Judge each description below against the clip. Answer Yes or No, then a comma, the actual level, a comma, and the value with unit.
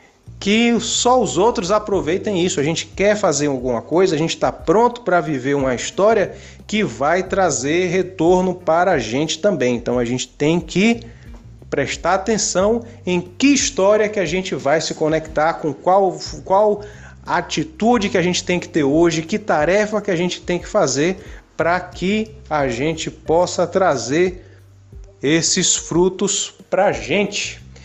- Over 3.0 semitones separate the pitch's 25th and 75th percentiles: Yes, average, 4.7 semitones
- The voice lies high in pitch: No, medium, 180 Hz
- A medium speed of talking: Yes, average, 160 wpm